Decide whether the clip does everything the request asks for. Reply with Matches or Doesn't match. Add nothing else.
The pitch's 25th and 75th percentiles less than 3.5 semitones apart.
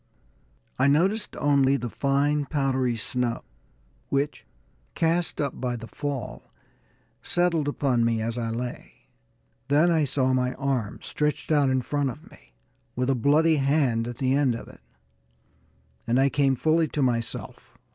Matches